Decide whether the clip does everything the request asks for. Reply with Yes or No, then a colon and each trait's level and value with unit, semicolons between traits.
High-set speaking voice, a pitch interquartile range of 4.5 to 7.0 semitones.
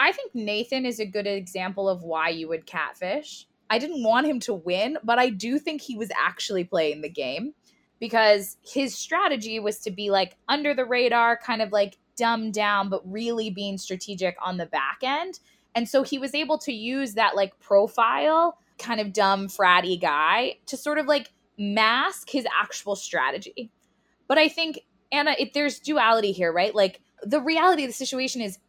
Yes: high, 225 Hz; wide, 5.6 semitones